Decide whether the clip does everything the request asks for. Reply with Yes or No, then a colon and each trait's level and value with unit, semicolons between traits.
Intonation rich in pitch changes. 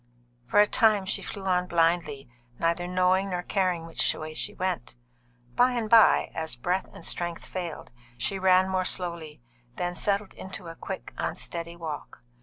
No: narrow, 2.4 semitones